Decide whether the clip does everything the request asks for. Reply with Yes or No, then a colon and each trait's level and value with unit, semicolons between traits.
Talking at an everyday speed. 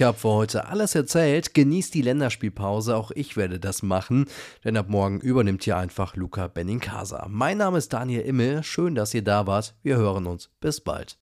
No: fast, 200 wpm